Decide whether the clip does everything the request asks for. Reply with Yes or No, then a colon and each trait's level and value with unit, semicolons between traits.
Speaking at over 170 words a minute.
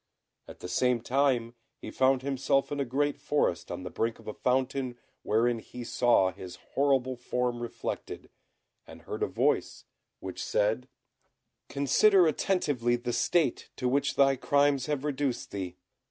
No: average, 155 wpm